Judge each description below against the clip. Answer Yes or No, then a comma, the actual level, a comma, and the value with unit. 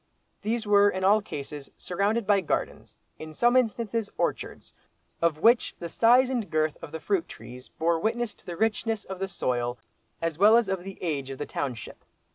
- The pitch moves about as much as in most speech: No, wide, 6.0 semitones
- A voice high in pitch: Yes, high, 195 Hz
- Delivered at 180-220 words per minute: Yes, average, 195 wpm